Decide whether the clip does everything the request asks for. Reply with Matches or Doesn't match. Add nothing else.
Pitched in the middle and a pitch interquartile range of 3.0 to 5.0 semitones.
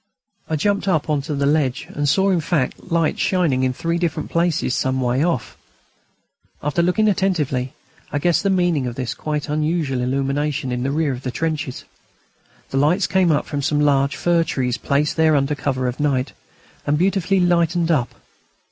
Matches